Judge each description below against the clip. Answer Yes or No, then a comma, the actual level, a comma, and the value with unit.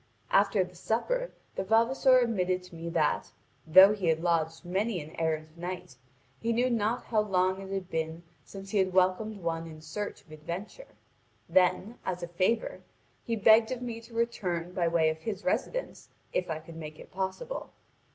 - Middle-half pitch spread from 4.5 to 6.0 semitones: Yes, average, 4.8 semitones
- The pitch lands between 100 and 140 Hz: No, medium, 185 Hz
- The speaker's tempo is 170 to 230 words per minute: Yes, average, 180 wpm